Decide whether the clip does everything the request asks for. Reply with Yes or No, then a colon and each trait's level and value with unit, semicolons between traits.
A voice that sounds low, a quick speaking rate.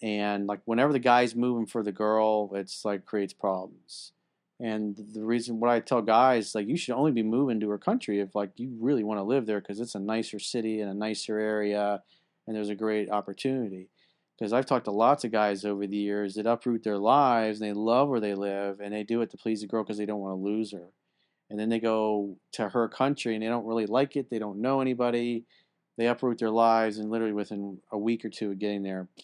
Yes: low, 110 Hz; fast, 240 wpm